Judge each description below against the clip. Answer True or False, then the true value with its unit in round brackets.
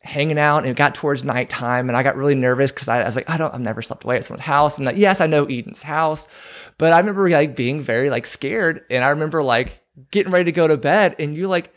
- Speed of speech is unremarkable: False (270 wpm)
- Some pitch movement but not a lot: True (3.8 semitones)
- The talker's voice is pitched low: False (145 Hz)